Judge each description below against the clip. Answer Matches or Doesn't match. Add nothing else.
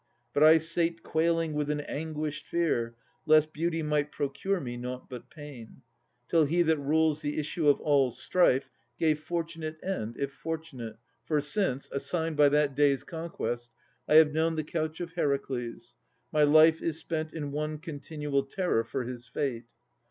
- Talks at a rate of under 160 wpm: Doesn't match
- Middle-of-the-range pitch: Matches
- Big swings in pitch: Doesn't match